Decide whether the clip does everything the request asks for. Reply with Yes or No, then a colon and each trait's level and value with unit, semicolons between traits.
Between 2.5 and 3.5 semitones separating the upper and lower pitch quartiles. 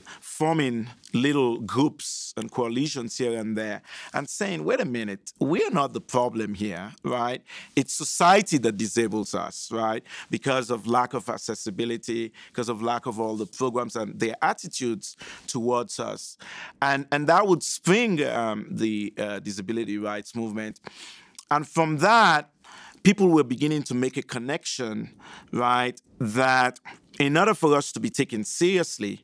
No: average, 4.4 semitones